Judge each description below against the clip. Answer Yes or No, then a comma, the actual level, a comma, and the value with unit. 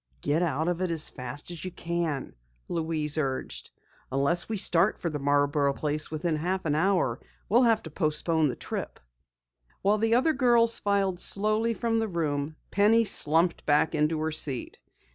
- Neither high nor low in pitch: Yes, medium, 165 Hz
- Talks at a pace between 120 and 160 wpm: No, average, 170 wpm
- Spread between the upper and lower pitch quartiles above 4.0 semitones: Yes, average, 5.0 semitones